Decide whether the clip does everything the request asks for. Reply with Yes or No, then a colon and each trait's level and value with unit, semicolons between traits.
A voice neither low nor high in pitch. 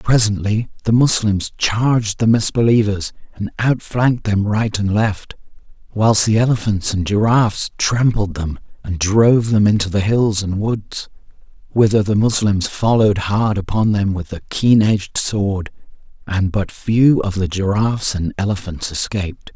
No: low, 105 Hz